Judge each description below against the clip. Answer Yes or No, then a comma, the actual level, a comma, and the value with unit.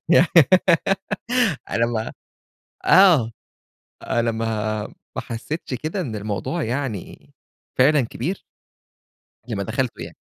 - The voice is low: Yes, low, 120 Hz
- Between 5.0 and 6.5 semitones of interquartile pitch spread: Yes, wide, 5.4 semitones